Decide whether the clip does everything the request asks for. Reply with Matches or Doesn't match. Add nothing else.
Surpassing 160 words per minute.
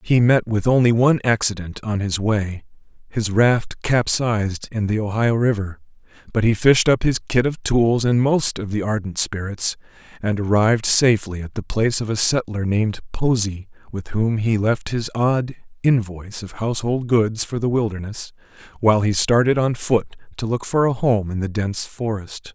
Matches